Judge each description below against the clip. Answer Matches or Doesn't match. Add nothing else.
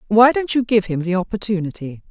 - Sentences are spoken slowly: Doesn't match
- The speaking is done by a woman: Matches